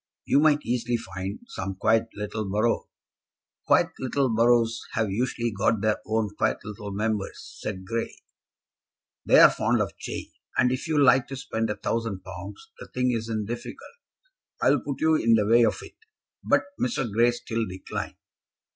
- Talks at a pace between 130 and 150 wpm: No, average, 165 wpm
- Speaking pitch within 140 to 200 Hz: No, low, 115 Hz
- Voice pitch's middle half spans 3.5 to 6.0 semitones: No, average, 2.7 semitones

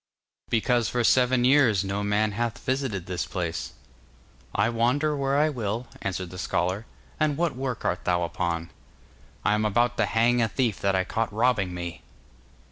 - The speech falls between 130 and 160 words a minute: No, average, 170 wpm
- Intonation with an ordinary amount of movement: Yes, average, 5.0 semitones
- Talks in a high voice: No, low, 110 Hz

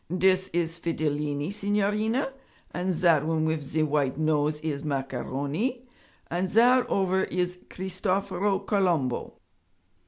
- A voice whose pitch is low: No, medium, 175 Hz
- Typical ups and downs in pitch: Yes, average, 4.4 semitones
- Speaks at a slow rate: Yes, slow, 115 wpm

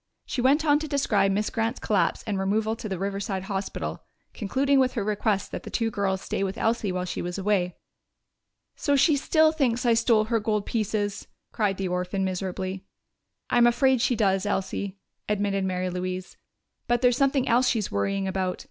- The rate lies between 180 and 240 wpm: Yes, average, 185 wpm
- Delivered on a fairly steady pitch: No, average, 3.9 semitones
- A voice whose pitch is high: Yes, high, 210 Hz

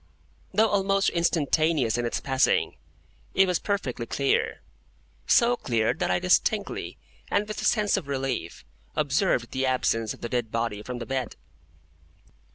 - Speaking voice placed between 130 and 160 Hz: Yes, medium, 140 Hz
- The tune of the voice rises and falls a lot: Yes, wide, 8.3 semitones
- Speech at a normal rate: Yes, average, 150 wpm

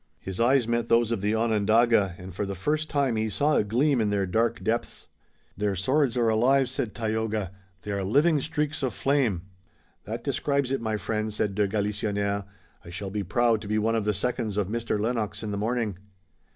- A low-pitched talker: Yes, low, 110 Hz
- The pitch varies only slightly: No, average, 3.0 semitones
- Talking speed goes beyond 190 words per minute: Yes, fast, 205 wpm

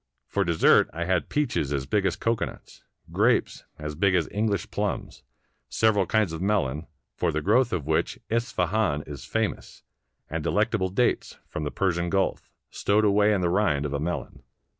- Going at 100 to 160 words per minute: No, average, 170 wpm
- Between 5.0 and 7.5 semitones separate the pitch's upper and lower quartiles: Yes, wide, 5.4 semitones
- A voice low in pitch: Yes, very low, 90 Hz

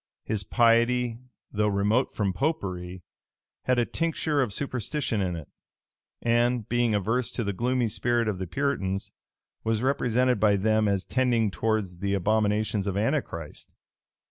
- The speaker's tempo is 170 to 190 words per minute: No, average, 145 wpm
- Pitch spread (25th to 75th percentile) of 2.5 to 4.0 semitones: Yes, average, 3.7 semitones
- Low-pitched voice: Yes, low, 110 Hz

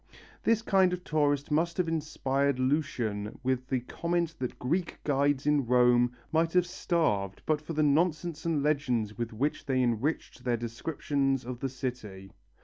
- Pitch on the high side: No, medium, 140 Hz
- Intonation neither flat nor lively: Yes, average, 4.5 semitones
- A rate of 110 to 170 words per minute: Yes, average, 160 wpm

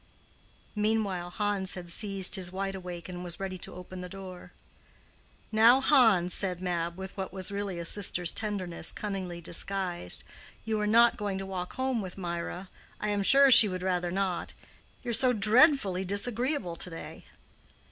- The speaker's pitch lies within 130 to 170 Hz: No, high, 190 Hz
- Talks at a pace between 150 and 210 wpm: Yes, average, 165 wpm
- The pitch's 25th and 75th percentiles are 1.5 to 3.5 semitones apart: Yes, average, 2.9 semitones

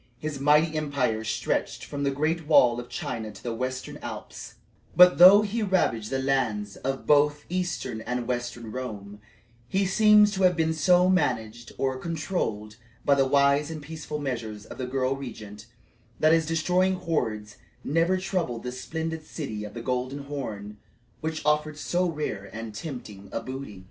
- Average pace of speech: Yes, average, 165 wpm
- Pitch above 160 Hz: No, medium, 140 Hz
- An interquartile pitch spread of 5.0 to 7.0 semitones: Yes, wide, 5.4 semitones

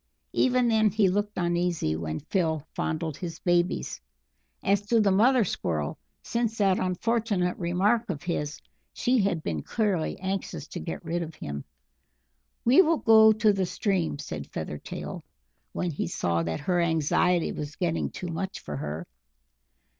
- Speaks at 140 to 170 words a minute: Yes, average, 155 wpm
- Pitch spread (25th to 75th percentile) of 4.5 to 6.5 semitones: Yes, average, 5.1 semitones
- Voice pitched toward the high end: No, medium, 180 Hz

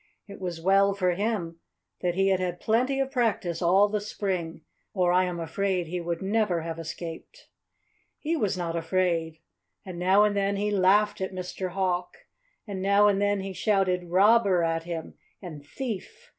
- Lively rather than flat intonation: No, average, 2.8 semitones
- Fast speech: No, average, 175 wpm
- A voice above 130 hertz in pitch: Yes, high, 190 Hz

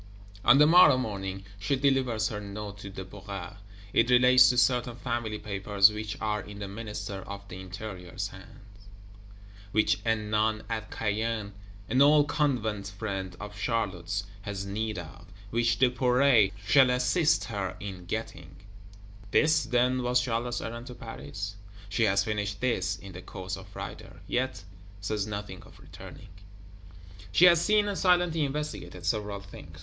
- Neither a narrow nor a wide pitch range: Yes, average, 3.8 semitones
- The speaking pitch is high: No, low, 105 Hz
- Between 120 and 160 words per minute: Yes, average, 150 wpm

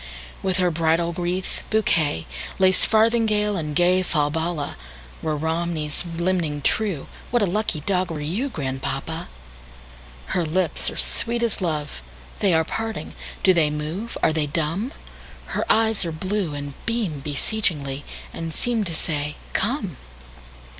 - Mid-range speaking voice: Yes, medium, 165 Hz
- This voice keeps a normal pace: No, slow, 105 wpm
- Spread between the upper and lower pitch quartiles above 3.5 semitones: Yes, average, 4.5 semitones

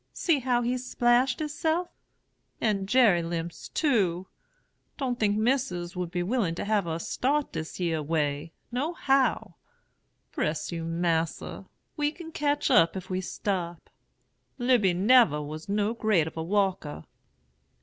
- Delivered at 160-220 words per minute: No, average, 140 wpm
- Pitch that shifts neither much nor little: No, wide, 7.0 semitones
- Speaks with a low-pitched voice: No, high, 200 Hz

